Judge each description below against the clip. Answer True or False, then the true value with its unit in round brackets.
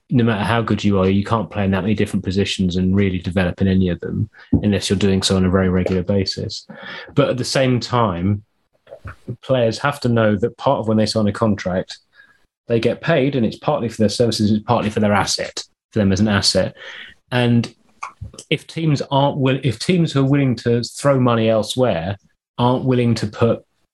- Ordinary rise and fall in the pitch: True (3.6 semitones)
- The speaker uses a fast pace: True (210 wpm)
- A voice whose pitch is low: True (110 Hz)